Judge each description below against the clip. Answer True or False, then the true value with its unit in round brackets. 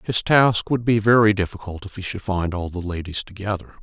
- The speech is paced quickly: True (220 wpm)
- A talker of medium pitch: False (100 Hz)